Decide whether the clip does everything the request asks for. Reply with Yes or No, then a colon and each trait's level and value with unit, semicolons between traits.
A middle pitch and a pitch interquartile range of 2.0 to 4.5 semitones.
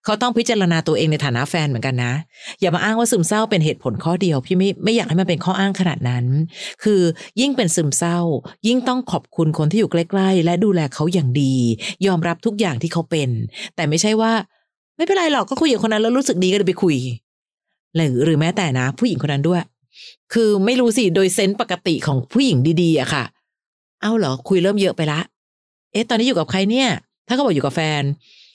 No: medium, 180 Hz; wide, 5.5 semitones